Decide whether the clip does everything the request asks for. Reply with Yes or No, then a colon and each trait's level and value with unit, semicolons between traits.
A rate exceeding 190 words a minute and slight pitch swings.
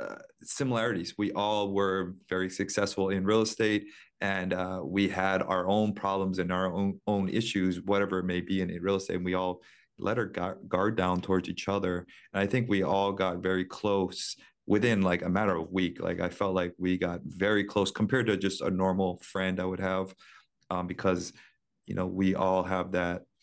Yes: average, 200 wpm; narrow, 1.5 semitones